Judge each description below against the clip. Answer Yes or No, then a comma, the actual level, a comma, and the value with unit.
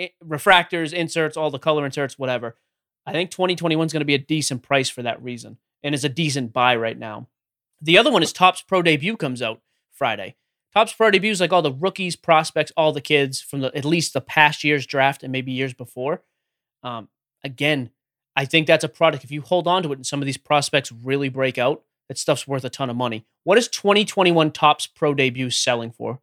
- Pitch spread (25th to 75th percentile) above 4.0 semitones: No, average, 3.7 semitones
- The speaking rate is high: Yes, fast, 220 wpm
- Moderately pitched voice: Yes, medium, 145 Hz